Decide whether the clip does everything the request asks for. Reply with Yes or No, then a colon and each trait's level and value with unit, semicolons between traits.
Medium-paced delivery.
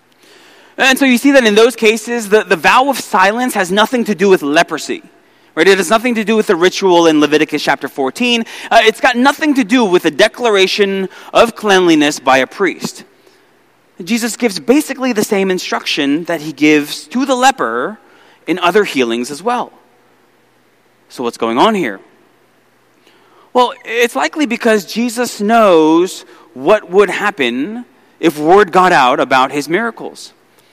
Yes: average, 165 wpm